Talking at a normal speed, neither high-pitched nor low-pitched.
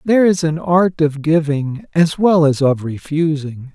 Yes: average, 175 wpm; medium, 155 Hz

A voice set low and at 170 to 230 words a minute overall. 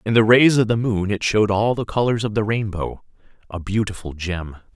Yes: low, 105 Hz; average, 200 wpm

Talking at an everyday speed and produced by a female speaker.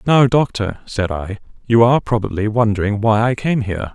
No: average, 185 wpm; male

